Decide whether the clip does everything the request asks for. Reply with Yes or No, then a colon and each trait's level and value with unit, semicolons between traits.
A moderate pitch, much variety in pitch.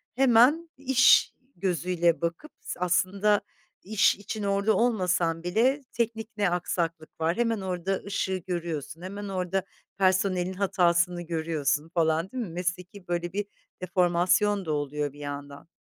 No: medium, 180 Hz; average, 3.3 semitones